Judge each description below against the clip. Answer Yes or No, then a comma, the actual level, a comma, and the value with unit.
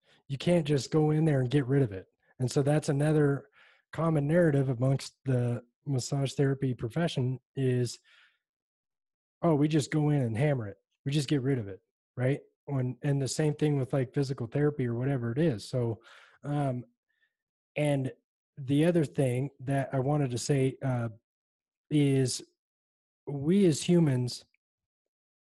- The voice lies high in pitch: No, medium, 140 Hz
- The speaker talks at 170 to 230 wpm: No, average, 160 wpm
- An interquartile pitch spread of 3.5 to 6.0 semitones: No, average, 2.8 semitones